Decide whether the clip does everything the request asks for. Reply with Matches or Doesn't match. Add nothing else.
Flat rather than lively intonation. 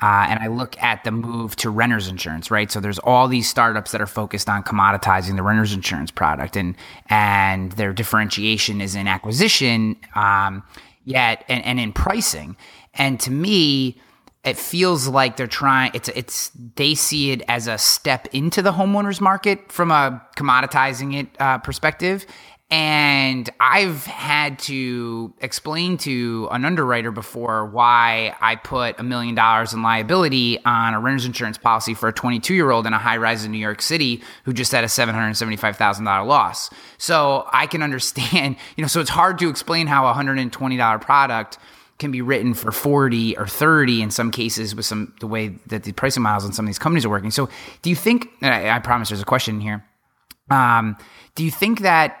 Doesn't match